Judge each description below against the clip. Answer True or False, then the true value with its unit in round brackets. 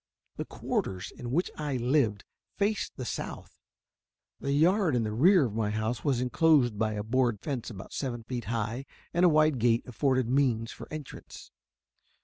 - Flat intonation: False (4.7 semitones)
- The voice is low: True (125 Hz)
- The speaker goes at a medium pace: True (170 wpm)